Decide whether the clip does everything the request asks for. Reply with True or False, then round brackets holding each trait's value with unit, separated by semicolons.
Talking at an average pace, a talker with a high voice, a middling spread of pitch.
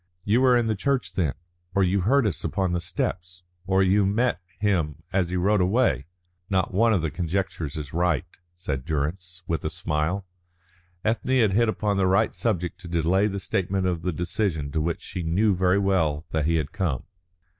False (195 wpm; 90 Hz; 3.4 semitones)